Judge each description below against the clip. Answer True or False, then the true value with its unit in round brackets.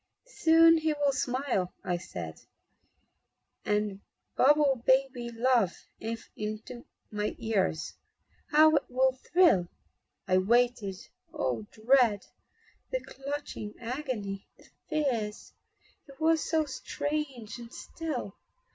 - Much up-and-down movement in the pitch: True (5.8 semitones)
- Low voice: False (245 Hz)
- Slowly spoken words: True (105 wpm)